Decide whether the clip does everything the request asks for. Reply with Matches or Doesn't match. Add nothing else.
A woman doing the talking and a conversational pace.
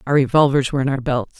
Doesn't match